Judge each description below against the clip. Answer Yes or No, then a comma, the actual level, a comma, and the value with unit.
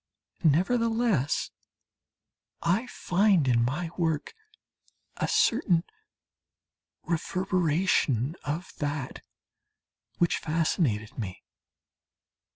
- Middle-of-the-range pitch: Yes, medium, 165 Hz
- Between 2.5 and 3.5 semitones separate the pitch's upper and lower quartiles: No, average, 4.5 semitones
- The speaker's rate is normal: No, slow, 65 wpm